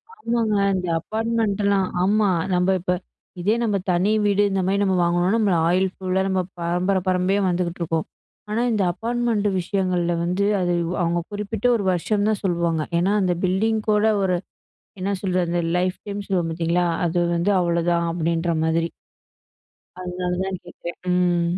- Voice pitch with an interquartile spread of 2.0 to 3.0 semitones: Yes, narrow, 2.6 semitones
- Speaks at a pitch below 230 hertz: Yes, medium, 185 Hz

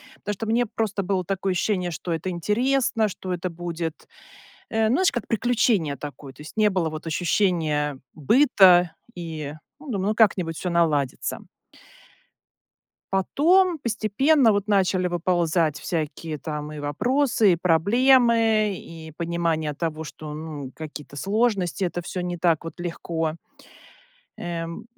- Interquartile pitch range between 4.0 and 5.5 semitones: Yes, average, 5.0 semitones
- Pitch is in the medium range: Yes, medium, 175 Hz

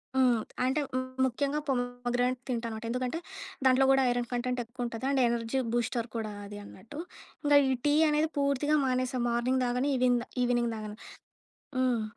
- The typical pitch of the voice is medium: No, very high, 250 Hz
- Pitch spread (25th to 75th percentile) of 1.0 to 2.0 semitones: Yes, narrow, 1.7 semitones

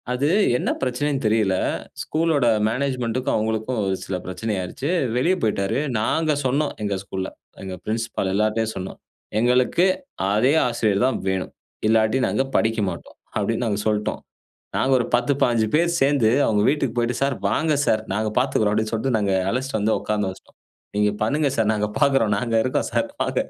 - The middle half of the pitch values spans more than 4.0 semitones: No, average, 3.7 semitones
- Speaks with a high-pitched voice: No, low, 115 Hz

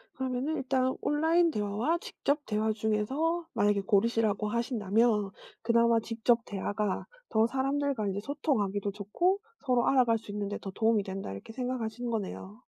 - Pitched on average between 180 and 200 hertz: No, high, 230 Hz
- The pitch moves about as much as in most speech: Yes, average, 4.2 semitones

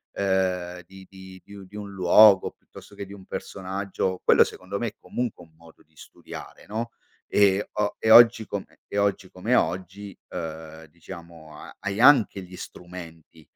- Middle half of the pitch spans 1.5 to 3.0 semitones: Yes, narrow, 2.5 semitones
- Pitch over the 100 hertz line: No, very low, 95 Hz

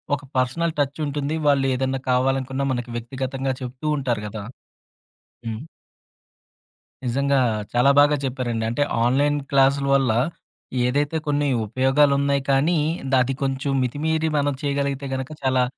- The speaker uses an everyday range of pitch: No, narrow, 1.9 semitones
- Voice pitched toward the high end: No, low, 135 Hz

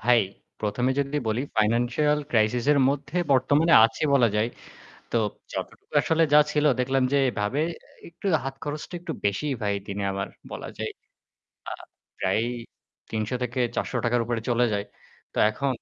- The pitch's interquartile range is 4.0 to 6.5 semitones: Yes, average, 4.5 semitones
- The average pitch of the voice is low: Yes, low, 125 Hz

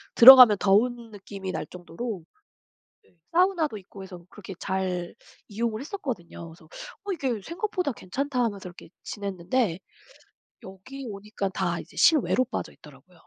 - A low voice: No, high, 210 Hz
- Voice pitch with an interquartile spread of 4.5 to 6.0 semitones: Yes, wide, 5.4 semitones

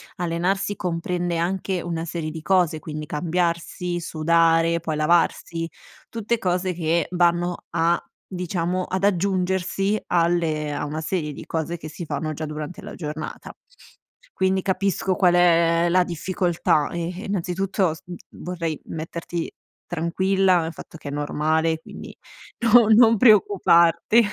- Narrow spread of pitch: Yes, narrow, 2.2 semitones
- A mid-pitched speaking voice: Yes, medium, 170 Hz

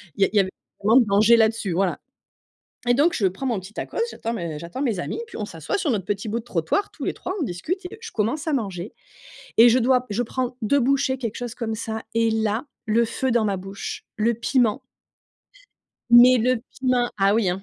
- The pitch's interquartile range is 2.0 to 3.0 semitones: No, average, 3.9 semitones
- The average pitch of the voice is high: Yes, high, 230 Hz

